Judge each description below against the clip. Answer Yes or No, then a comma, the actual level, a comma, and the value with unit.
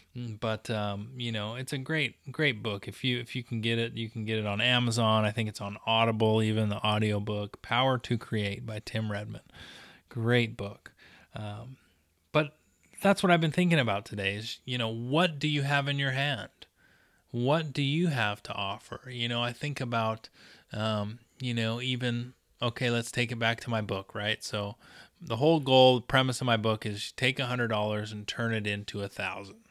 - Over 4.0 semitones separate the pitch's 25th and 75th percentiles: No, average, 3.3 semitones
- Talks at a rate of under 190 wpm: No, fast, 205 wpm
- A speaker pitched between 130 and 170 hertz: No, low, 115 Hz